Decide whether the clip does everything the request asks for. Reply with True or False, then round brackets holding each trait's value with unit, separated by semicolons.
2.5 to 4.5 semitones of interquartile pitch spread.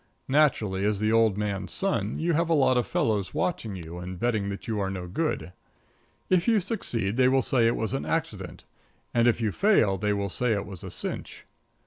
False (5.2 semitones)